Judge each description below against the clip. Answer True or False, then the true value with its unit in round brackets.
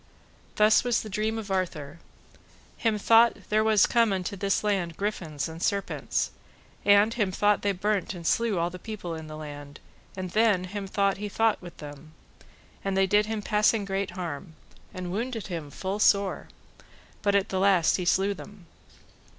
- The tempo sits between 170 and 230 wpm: True (175 wpm)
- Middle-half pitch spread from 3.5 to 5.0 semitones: False (3.1 semitones)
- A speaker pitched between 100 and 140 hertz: False (195 Hz)